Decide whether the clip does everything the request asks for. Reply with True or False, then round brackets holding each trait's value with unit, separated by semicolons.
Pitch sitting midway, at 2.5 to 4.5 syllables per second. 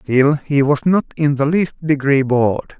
True (145 Hz; 4.3 syllables/s)